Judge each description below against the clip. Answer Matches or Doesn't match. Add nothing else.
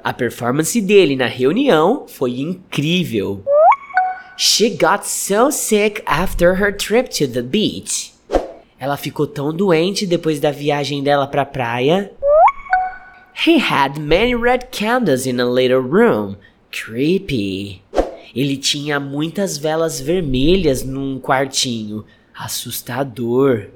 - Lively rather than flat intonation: Matches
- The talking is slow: Matches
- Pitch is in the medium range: Matches